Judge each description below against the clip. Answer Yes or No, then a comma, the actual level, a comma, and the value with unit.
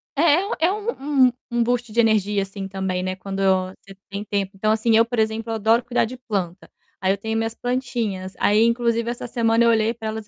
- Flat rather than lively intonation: No, average, 3.2 semitones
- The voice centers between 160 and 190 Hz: No, high, 225 Hz